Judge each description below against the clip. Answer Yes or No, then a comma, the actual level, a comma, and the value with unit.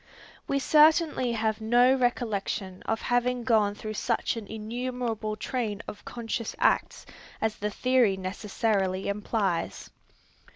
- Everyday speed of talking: No, slow, 120 wpm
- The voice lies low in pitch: No, high, 225 Hz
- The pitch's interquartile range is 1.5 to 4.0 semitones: Yes, average, 2.9 semitones